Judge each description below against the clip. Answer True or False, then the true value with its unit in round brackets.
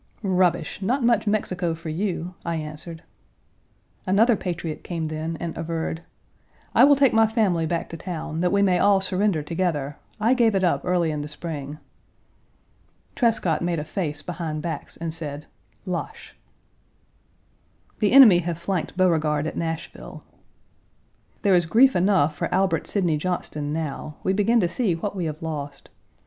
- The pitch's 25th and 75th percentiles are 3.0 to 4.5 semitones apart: True (3.7 semitones)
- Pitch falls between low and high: True (175 Hz)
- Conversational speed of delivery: True (160 wpm)